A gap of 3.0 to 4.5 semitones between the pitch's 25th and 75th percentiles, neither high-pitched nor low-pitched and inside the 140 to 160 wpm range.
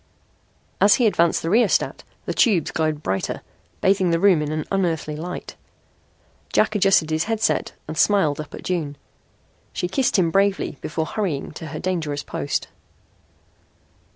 Yes: average, 4.1 semitones; medium, 170 Hz; average, 145 wpm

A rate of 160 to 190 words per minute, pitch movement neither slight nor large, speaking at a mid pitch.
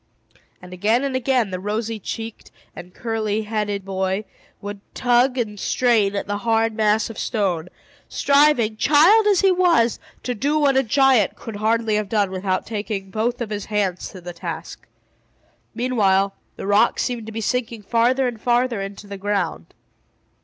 No: average, 170 wpm; average, 3.5 semitones; high, 220 Hz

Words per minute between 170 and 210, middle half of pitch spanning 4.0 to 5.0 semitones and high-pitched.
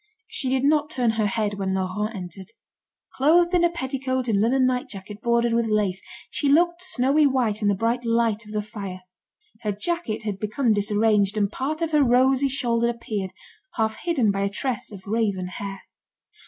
Yes: average, 185 wpm; average, 4.4 semitones; high, 230 Hz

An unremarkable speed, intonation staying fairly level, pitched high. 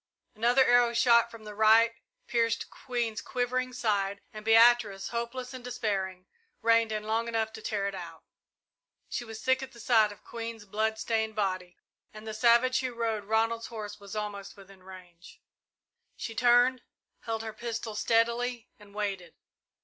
Yes: average, 160 wpm; narrow, 2.2 semitones; high, 225 Hz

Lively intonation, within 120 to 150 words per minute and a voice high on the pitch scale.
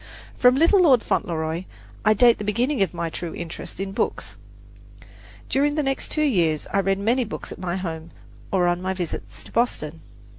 No: wide, 6.5 semitones; average, 185 wpm; high, 195 Hz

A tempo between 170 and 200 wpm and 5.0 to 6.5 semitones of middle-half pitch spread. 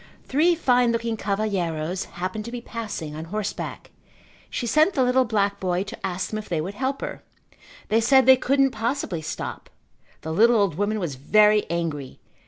Yes: average, 180 wpm; wide, 5.5 semitones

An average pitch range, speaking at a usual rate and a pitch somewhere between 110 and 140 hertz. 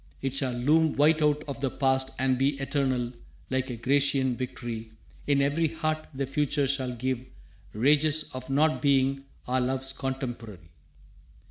No: narrow, 1.9 semitones; average, 150 wpm; low, 135 Hz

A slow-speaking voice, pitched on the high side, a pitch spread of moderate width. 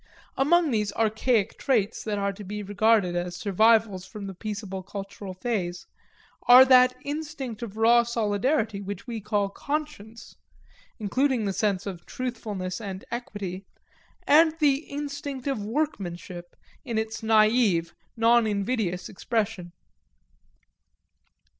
Yes: slow, 120 wpm; high, 215 Hz; average, 3.8 semitones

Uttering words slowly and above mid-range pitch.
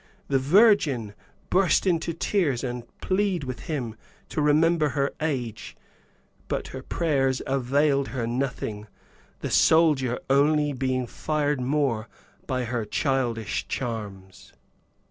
No: slow, 120 wpm; low, 135 Hz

